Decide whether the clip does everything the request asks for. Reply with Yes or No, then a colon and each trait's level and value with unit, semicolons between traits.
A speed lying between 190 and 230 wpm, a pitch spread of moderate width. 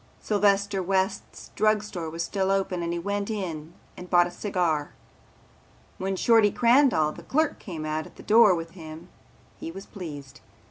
No: average, 170 wpm; average, 3.6 semitones